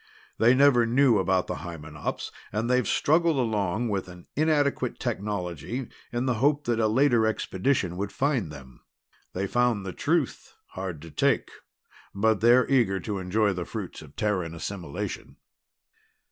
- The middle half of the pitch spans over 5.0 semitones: Yes, wide, 5.6 semitones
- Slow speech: No, average, 150 wpm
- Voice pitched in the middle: No, low, 110 Hz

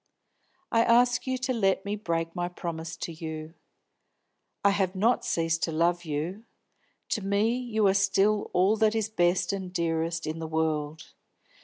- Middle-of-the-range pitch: Yes, medium, 180 Hz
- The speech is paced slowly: No, average, 165 wpm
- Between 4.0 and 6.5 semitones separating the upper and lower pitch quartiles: Yes, average, 4.5 semitones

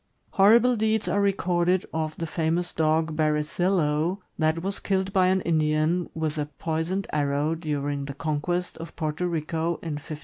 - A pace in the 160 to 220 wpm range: Yes, average, 165 wpm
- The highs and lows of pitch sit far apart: No, average, 3.0 semitones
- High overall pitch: No, medium, 165 Hz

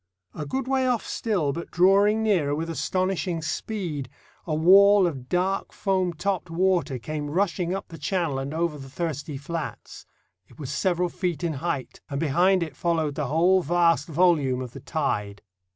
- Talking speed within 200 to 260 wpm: No, average, 170 wpm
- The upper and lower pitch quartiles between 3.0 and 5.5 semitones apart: Yes, average, 4.1 semitones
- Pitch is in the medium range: Yes, medium, 170 Hz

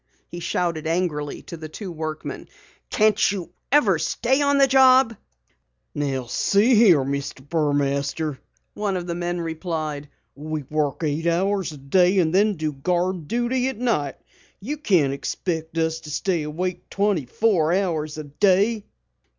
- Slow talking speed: No, average, 150 wpm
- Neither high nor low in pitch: Yes, medium, 170 Hz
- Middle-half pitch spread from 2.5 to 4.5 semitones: No, average, 4.9 semitones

